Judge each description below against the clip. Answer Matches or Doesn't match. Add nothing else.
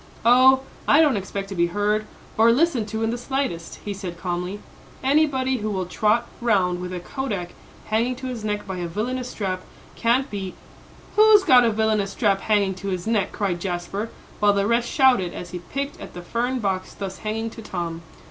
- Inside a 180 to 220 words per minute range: Matches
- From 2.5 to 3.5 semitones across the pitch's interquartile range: Doesn't match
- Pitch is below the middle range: Doesn't match